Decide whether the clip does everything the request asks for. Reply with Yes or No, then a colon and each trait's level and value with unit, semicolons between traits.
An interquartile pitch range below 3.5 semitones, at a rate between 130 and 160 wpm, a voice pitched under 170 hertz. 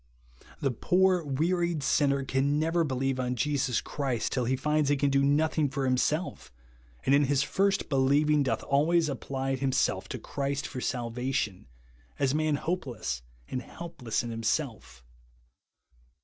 Yes: average, 2.9 semitones; average, 150 wpm; medium, 140 Hz